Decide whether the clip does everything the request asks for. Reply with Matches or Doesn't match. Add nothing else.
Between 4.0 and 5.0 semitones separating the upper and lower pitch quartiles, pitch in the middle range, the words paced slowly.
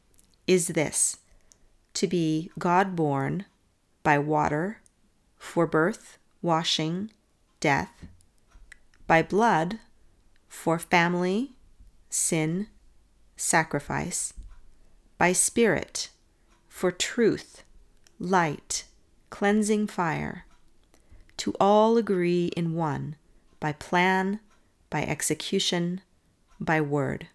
Matches